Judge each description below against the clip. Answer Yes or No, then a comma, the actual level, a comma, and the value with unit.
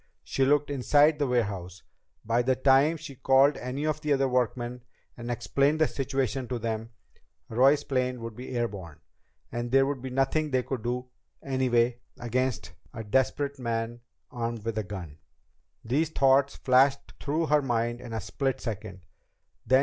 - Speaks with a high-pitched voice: No, low, 125 Hz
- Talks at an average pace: Yes, average, 165 wpm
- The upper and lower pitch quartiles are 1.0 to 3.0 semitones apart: Yes, average, 2.7 semitones